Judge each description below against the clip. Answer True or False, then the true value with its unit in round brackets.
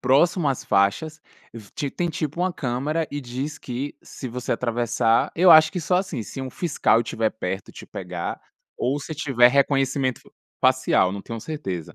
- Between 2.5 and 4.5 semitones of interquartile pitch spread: False (4.9 semitones)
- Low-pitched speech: True (130 Hz)